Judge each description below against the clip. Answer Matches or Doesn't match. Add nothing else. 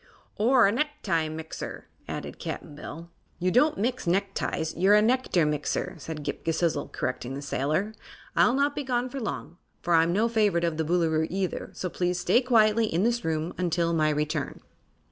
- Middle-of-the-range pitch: Matches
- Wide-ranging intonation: Matches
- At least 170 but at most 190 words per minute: Matches